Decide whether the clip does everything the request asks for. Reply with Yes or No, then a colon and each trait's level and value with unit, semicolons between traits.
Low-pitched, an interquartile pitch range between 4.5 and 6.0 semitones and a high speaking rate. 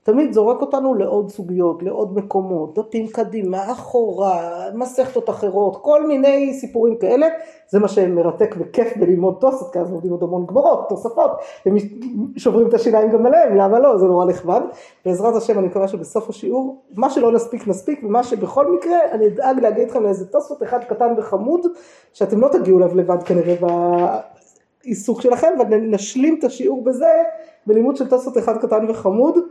No: high, 225 Hz; average, 5.2 semitones; fast, 160 wpm